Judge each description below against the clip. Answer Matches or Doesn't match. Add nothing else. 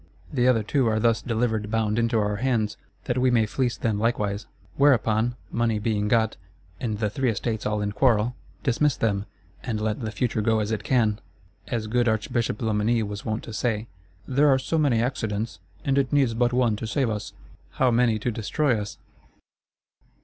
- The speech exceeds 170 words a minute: Matches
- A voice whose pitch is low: Matches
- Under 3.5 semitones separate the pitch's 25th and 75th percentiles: Matches